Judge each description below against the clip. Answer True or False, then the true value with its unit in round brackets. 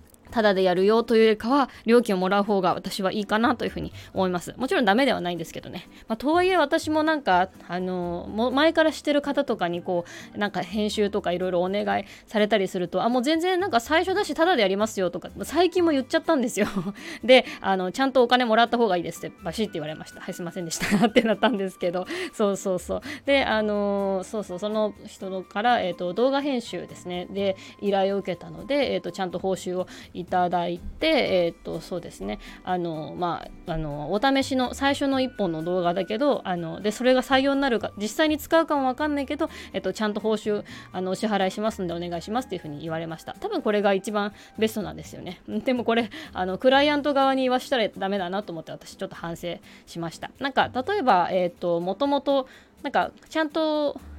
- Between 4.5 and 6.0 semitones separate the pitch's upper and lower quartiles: False (6.4 semitones)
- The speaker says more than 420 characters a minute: True (450 characters per minute)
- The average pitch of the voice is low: False (210 Hz)